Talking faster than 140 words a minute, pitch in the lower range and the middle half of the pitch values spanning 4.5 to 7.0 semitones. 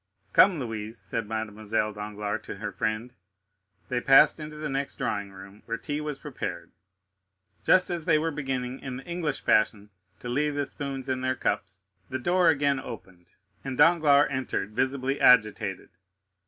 Yes: average, 160 wpm; low, 130 Hz; average, 5.3 semitones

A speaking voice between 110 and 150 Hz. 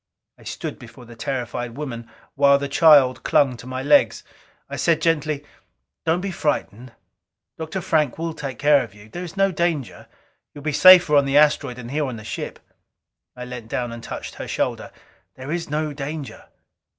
Yes: medium, 140 Hz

